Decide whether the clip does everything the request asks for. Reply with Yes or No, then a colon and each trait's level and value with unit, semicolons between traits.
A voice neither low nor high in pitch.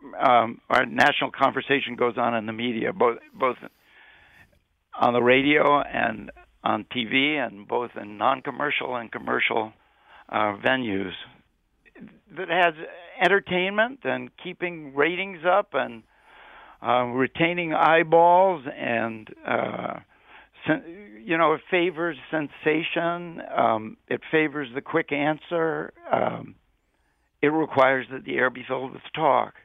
Yes: medium, 145 Hz